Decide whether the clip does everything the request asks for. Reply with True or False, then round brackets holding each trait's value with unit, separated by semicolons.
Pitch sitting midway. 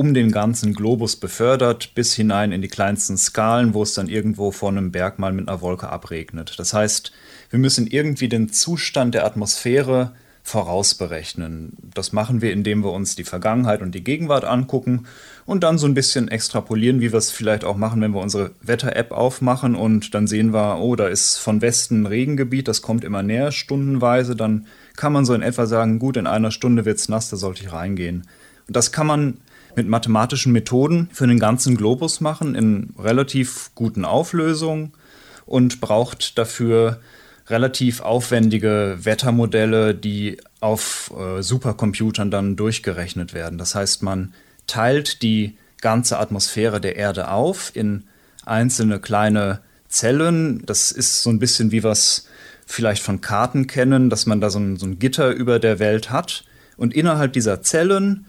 False (110 Hz)